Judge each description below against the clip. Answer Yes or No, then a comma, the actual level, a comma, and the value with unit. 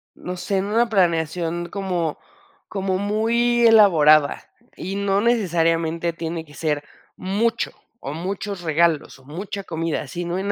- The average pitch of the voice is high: No, medium, 175 Hz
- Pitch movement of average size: Yes, average, 3.6 semitones